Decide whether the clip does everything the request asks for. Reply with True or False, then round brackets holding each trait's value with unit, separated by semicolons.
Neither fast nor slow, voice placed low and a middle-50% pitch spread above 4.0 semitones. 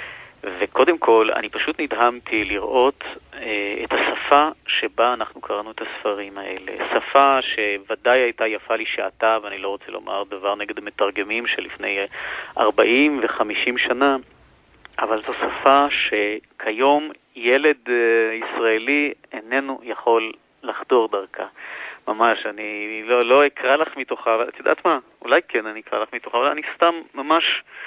True (135 wpm; 115 Hz; 4.6 semitones)